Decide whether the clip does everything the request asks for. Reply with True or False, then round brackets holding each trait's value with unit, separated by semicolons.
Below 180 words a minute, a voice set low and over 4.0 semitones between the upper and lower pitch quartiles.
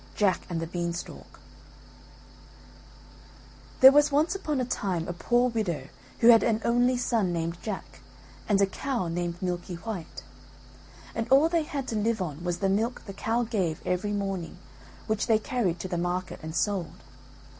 False (165 wpm; 200 Hz; 5.2 semitones)